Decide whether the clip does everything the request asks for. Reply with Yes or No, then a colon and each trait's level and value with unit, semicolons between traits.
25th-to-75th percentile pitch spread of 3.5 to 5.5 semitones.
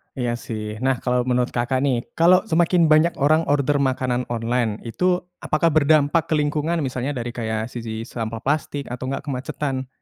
Yes: average, 4.0 semitones